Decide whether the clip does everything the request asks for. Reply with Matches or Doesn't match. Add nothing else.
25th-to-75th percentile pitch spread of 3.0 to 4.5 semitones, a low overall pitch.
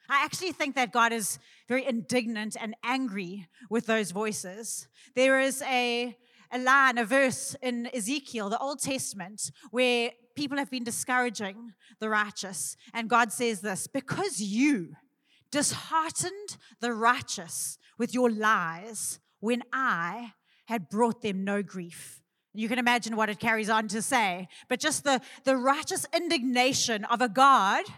Doesn't match